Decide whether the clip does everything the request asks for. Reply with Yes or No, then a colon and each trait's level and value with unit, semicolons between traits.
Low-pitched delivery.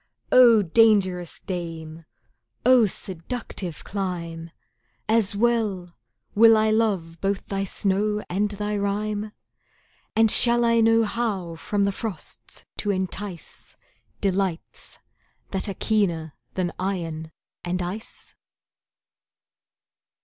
No: high, 200 Hz